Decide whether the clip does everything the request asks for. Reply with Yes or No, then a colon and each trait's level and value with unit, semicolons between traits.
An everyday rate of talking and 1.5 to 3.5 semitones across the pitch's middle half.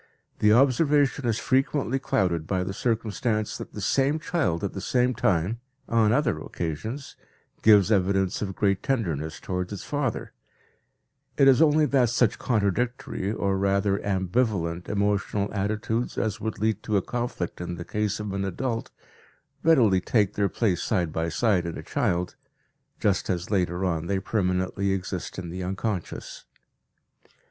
No: average, 155 wpm; average, 4.3 semitones